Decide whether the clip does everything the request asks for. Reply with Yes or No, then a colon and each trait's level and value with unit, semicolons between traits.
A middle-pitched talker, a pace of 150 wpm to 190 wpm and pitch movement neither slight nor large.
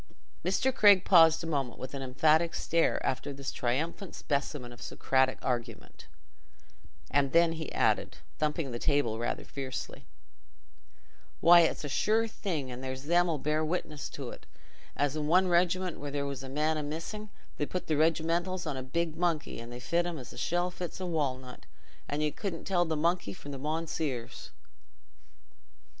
Yes: medium, 155 Hz; average, 170 wpm; average, 4.1 semitones